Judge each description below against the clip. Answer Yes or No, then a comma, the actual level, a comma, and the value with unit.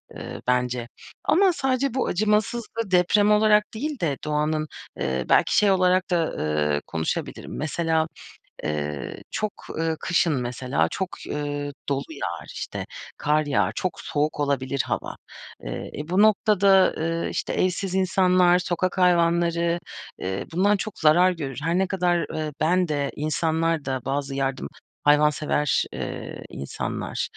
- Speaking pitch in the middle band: Yes, medium, 165 Hz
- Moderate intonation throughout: Yes, average, 4.4 semitones